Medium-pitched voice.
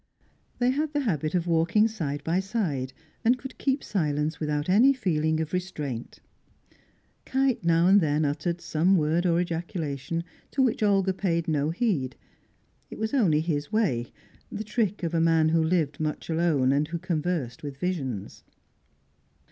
Yes: medium, 165 Hz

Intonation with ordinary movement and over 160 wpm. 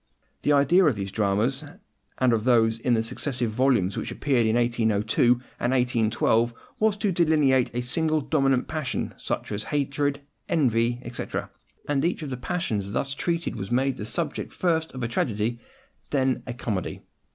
Yes: average, 4.0 semitones; average, 170 wpm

